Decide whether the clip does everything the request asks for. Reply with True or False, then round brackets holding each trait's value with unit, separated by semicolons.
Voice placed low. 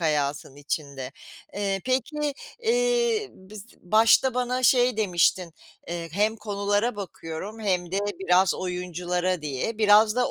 False (200 Hz)